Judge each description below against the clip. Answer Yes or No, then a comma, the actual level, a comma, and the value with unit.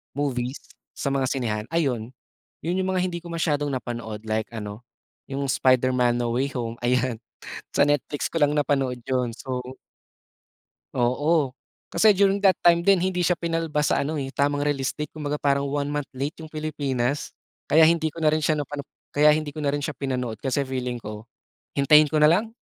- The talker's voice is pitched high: No, medium, 140 Hz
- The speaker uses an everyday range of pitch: Yes, average, 3.4 semitones